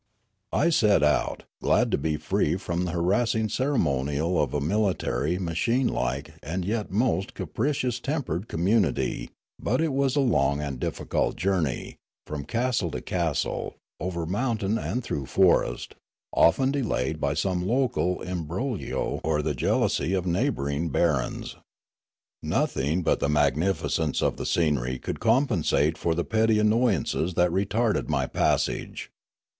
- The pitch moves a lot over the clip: Yes, wide, 6.8 semitones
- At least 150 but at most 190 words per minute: No, average, 140 wpm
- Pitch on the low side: Yes, very low, 90 Hz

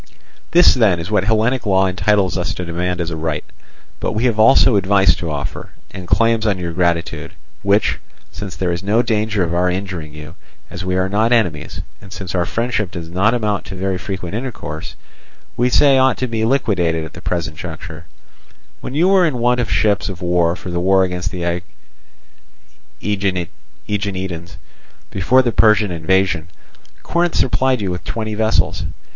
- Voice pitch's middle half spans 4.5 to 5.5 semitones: No, average, 4.1 semitones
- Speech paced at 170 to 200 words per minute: Yes, average, 175 wpm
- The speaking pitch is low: Yes, very low, 95 Hz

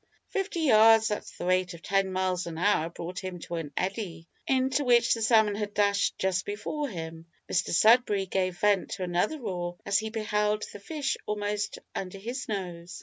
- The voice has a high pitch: Yes, high, 200 Hz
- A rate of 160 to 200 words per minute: Yes, average, 185 wpm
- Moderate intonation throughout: Yes, average, 3.4 semitones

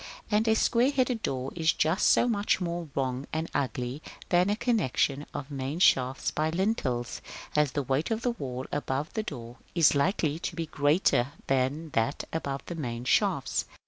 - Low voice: No, medium, 150 Hz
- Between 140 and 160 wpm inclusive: No, average, 175 wpm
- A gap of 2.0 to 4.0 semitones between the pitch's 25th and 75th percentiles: No, average, 5.2 semitones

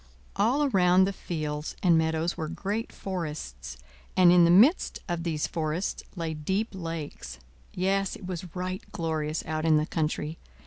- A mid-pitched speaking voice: Yes, medium, 170 Hz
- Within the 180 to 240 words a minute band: No, average, 160 wpm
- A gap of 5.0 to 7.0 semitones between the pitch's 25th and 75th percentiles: No, average, 3.1 semitones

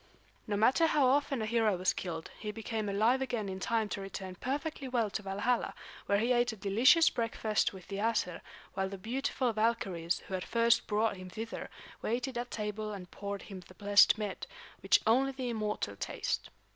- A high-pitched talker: Yes, high, 215 Hz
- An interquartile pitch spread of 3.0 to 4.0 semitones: Yes, average, 3.5 semitones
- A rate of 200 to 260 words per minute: No, average, 185 wpm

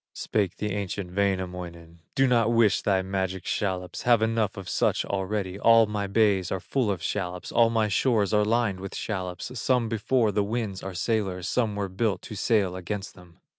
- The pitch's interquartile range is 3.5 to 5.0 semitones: No, average, 3.0 semitones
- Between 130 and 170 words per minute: No, average, 185 wpm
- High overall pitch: No, low, 100 Hz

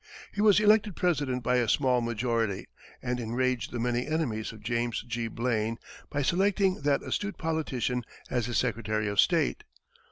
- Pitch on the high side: No, low, 125 Hz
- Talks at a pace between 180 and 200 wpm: No, average, 160 wpm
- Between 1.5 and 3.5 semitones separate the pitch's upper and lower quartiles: No, wide, 5.4 semitones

